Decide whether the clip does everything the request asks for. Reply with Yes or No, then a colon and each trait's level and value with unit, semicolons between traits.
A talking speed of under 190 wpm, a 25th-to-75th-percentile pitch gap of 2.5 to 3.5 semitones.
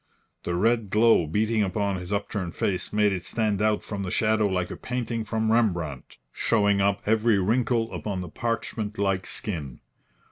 Yes: average, 170 wpm; average, 2.9 semitones